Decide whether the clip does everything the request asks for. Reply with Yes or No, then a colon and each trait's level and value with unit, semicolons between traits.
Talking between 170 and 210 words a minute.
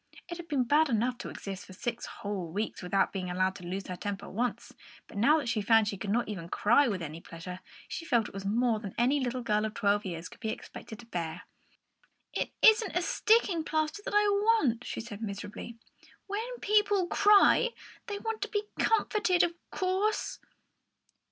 Yes: average, 195 wpm